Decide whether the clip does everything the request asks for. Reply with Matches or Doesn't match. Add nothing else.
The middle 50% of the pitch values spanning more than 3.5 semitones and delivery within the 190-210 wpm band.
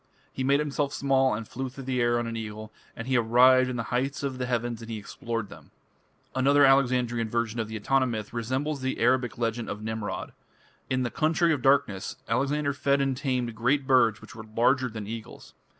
Doesn't match